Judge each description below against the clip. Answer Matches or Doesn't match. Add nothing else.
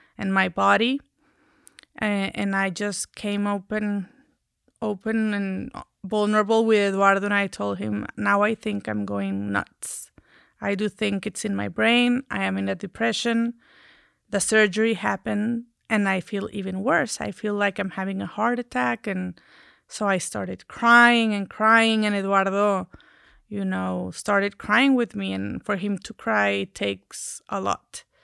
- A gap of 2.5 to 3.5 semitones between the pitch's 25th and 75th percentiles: Matches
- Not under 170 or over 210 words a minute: Doesn't match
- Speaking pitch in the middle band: Doesn't match